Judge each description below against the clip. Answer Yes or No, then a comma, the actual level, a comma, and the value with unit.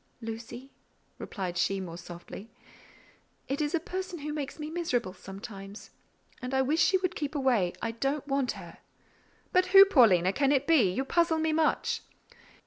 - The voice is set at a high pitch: Yes, very high, 270 Hz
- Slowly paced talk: No, average, 160 wpm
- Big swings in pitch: Yes, wide, 7.5 semitones